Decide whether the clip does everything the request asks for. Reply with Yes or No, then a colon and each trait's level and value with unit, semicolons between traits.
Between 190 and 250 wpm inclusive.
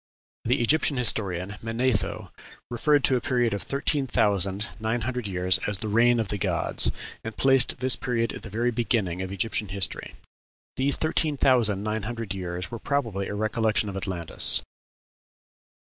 No: average, 160 wpm